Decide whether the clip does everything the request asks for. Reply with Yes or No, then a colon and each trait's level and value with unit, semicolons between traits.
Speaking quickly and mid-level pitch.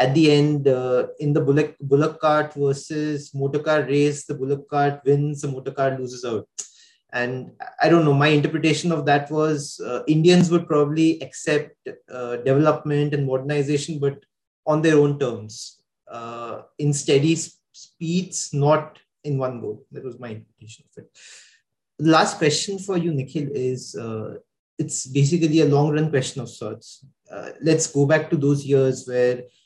Yes: fast, 165 wpm; medium, 145 Hz